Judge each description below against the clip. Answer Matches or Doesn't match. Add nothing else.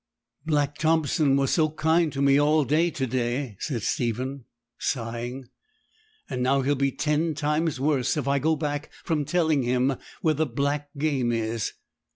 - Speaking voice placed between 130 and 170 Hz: Matches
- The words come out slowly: Doesn't match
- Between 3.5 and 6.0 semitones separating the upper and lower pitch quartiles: Doesn't match